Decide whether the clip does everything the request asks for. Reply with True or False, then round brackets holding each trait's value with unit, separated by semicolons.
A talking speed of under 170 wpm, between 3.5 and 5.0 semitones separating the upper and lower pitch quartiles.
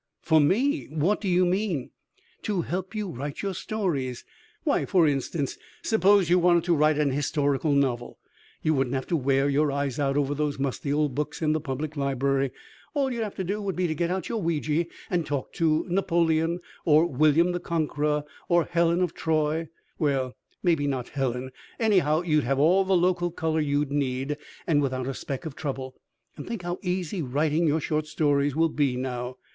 False (190 wpm; 3.8 semitones)